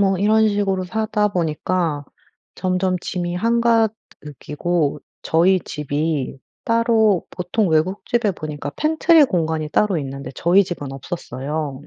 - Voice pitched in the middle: Yes, medium, 180 Hz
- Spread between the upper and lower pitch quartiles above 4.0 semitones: Yes, wide, 5.4 semitones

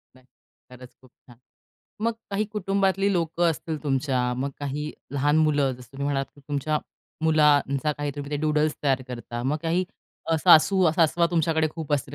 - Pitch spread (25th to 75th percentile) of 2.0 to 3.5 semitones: Yes, average, 3.0 semitones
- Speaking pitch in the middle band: Yes, medium, 150 Hz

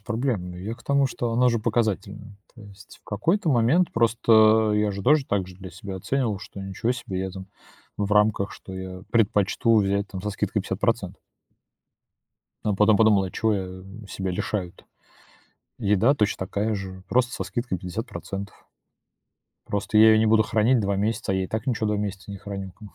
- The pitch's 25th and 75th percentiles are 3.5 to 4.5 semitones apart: No, narrow, 2.6 semitones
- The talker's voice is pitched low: Yes, low, 105 Hz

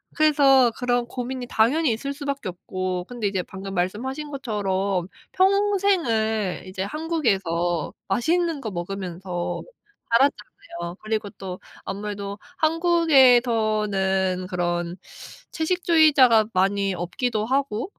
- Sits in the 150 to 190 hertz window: No, high, 220 Hz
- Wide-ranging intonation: Yes, wide, 6.5 semitones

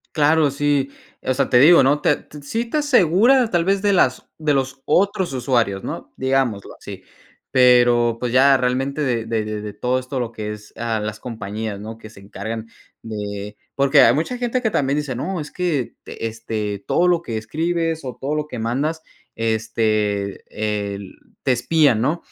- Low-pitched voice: Yes, low, 130 Hz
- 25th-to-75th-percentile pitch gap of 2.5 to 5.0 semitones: No, wide, 5.5 semitones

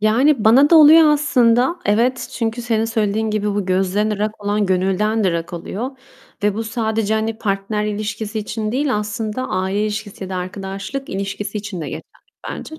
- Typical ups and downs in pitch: No, narrow, 2.2 semitones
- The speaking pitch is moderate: No, high, 215 Hz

